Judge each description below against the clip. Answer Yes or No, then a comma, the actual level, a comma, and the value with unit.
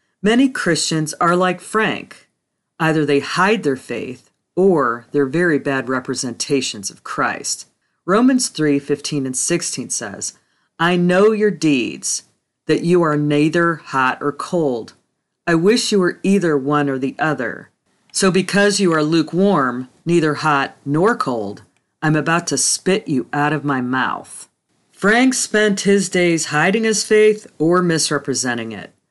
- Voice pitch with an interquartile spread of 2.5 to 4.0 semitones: No, average, 5.1 semitones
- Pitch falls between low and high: Yes, medium, 160 Hz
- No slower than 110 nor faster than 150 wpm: Yes, average, 145 wpm